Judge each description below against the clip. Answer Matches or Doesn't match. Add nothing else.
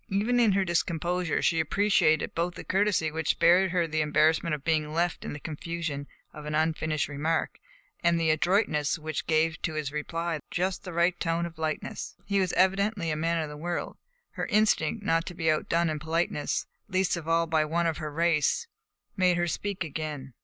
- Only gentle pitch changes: Matches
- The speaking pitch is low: Doesn't match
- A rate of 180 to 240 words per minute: Matches